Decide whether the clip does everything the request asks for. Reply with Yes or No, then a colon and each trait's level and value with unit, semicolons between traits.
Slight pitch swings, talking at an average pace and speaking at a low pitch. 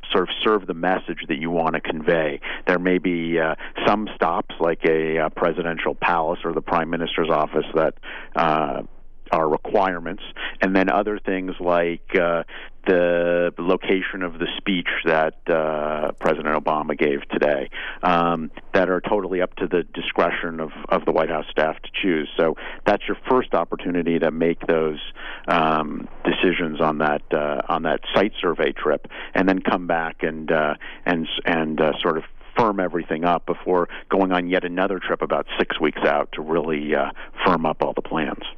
Yes: narrow, 2.0 semitones; average, 175 wpm; very low, 85 Hz